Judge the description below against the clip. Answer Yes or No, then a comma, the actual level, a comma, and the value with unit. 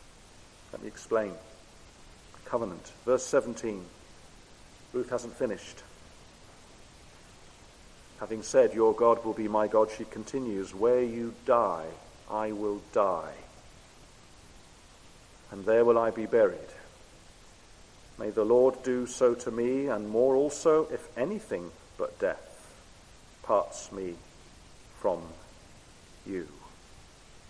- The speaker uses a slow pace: Yes, slow, 105 wpm